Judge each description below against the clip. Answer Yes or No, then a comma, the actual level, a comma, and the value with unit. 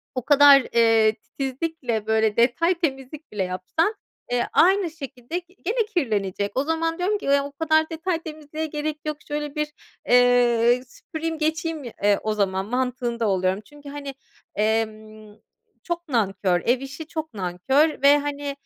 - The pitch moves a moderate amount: No, wide, 6.1 semitones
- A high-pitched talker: Yes, very high, 275 Hz